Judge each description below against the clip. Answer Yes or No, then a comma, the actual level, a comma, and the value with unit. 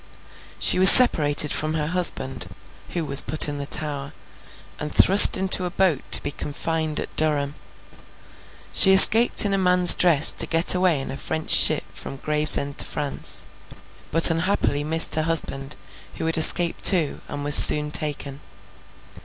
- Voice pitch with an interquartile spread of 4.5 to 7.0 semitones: No, average, 3.4 semitones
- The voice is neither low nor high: Yes, medium, 155 Hz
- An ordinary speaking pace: Yes, average, 160 wpm